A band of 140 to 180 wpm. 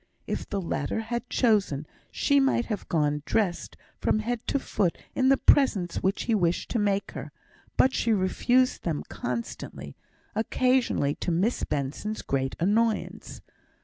Yes: average, 145 wpm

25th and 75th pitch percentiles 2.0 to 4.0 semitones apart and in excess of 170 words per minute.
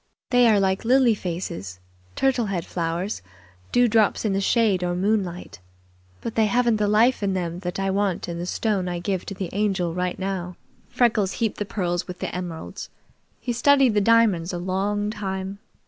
Yes: average, 3.5 semitones; average, 180 wpm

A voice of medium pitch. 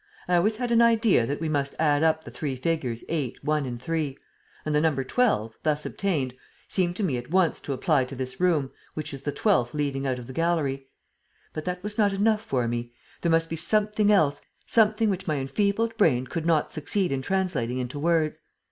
Yes: medium, 155 Hz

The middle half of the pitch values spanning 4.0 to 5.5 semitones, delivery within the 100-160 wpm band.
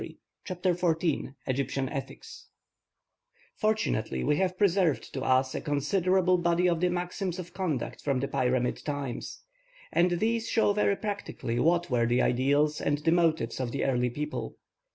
Yes: average, 5.2 semitones; average, 155 wpm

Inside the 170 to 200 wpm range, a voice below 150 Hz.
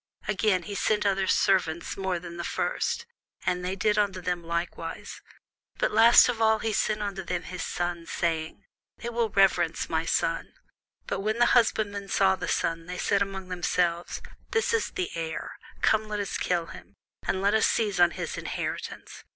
No: average, 180 wpm; high, 190 Hz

